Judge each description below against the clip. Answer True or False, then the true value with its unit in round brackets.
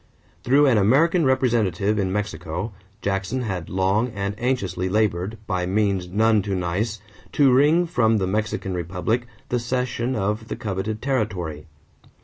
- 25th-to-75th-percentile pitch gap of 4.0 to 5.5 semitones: True (4.3 semitones)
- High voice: False (105 Hz)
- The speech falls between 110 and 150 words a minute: True (140 wpm)